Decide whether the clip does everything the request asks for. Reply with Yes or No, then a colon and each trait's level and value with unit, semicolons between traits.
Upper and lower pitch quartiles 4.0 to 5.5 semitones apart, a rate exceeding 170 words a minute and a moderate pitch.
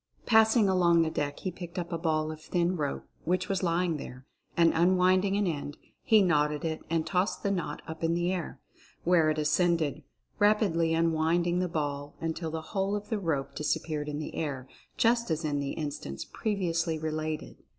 No: average, 2.8 semitones; average, 190 wpm; medium, 165 Hz